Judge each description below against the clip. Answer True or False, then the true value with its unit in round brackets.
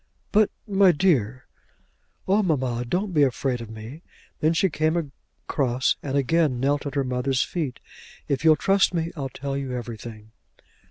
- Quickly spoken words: False (165 wpm)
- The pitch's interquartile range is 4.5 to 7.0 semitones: True (4.8 semitones)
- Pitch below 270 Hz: True (140 Hz)